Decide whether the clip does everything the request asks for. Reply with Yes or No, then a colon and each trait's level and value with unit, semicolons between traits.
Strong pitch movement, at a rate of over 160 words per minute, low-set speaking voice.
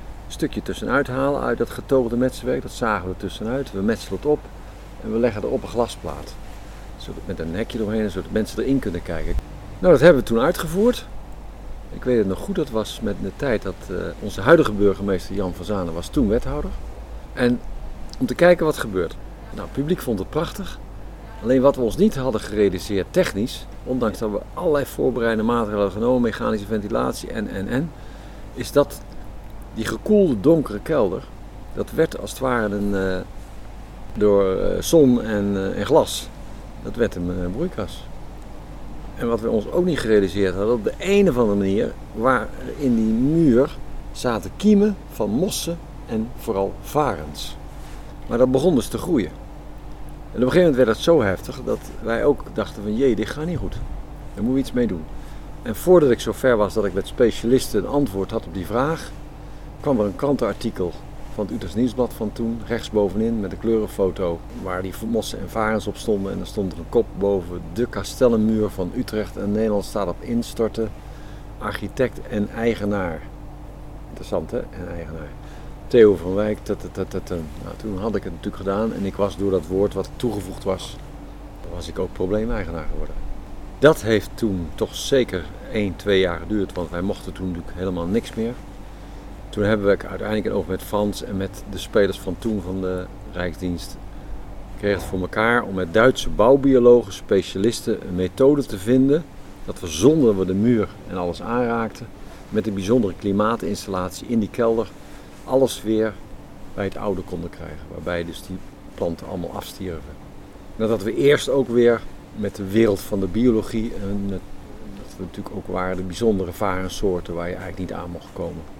No: average, 3.9 semitones; average, 180 wpm; low, 105 Hz